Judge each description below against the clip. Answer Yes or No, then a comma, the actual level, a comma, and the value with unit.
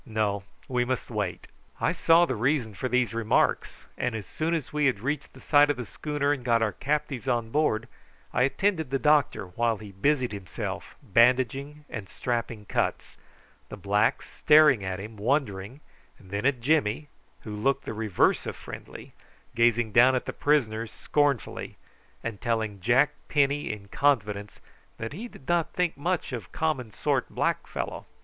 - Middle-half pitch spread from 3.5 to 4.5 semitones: No, average, 5.0 semitones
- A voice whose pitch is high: No, low, 125 Hz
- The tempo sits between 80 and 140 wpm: No, average, 170 wpm